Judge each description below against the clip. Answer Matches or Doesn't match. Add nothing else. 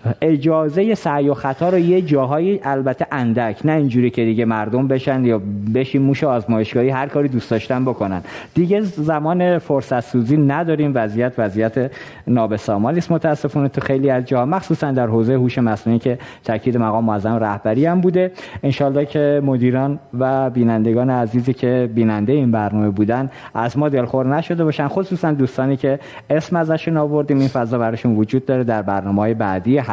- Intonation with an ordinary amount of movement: Matches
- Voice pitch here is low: Matches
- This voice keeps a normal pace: Doesn't match